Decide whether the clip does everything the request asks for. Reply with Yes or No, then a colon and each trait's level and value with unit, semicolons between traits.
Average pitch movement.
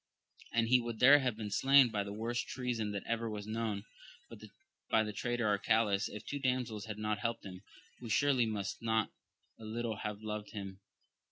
No: narrow, 2.2 semitones